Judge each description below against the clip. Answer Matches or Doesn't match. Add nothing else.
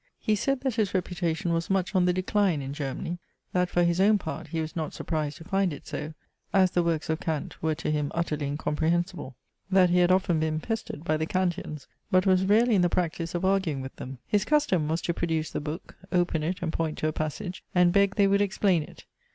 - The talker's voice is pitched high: Doesn't match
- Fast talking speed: Matches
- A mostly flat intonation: Doesn't match